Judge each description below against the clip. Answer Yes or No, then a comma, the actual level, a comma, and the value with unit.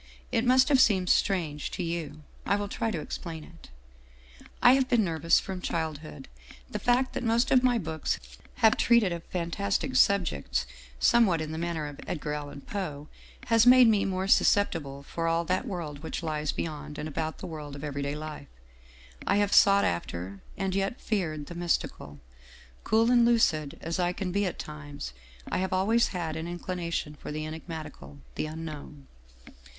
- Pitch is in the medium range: Yes, medium, 170 Hz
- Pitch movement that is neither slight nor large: Yes, average, 4.9 semitones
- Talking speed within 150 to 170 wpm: No, average, 180 wpm